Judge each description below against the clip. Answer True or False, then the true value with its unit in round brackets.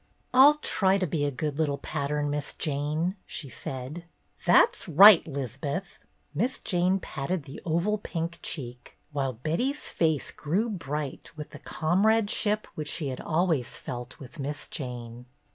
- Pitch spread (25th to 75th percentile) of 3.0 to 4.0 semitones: False (4.8 semitones)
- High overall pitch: False (155 Hz)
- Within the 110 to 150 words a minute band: True (145 wpm)